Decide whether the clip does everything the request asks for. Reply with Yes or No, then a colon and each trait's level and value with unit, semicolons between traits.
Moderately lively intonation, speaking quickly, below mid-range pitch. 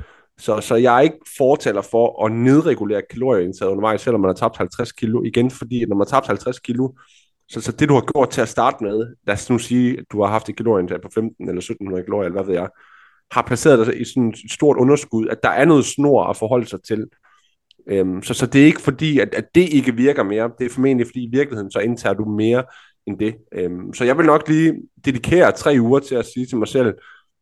Yes: average, 3.1 semitones; fast, 245 wpm; low, 120 Hz